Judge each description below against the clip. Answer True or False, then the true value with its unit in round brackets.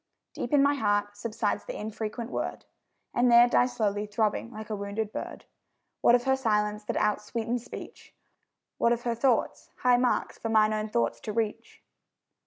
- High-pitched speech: True (220 Hz)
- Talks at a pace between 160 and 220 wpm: True (175 wpm)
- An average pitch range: False (2.3 semitones)